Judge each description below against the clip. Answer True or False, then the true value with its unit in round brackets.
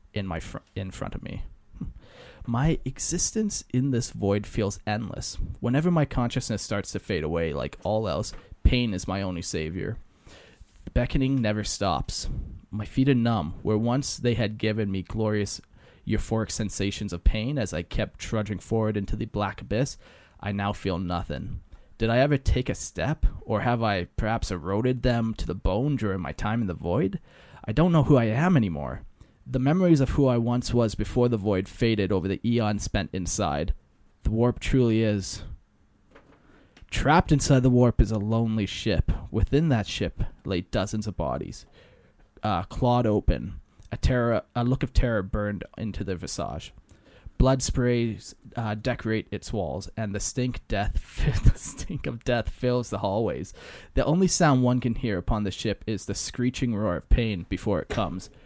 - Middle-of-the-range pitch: False (110 Hz)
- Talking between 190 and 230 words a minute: False (175 wpm)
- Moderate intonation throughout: True (4.2 semitones)